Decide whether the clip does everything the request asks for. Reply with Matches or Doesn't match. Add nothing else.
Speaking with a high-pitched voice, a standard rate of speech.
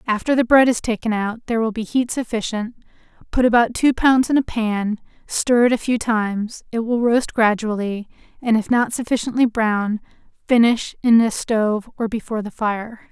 Matches